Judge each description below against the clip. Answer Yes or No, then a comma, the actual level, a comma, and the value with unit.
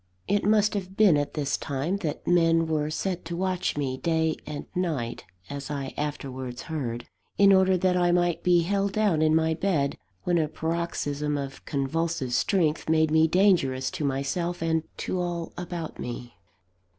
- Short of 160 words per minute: No, average, 170 wpm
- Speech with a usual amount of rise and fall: Yes, average, 3.7 semitones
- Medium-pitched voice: Yes, medium, 160 Hz